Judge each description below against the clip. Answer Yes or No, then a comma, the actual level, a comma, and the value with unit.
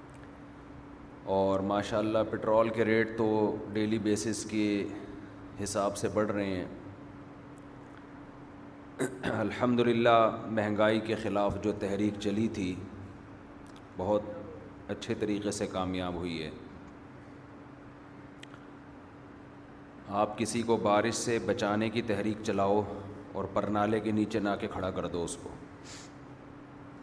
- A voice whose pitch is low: Yes, low, 105 Hz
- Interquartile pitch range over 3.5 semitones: No, average, 2.8 semitones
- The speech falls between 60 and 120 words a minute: Yes, average, 115 wpm